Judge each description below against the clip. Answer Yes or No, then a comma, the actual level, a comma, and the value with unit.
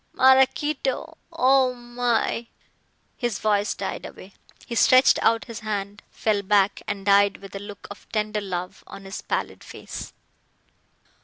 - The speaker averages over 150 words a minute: No, average, 145 wpm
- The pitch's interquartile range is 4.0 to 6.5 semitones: No, average, 3.6 semitones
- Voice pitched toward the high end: Yes, high, 215 Hz